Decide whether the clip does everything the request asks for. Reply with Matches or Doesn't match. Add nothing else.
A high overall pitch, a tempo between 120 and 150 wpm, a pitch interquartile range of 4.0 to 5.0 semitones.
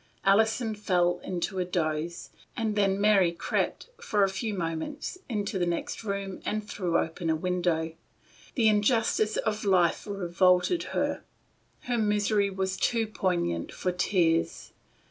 Doesn't match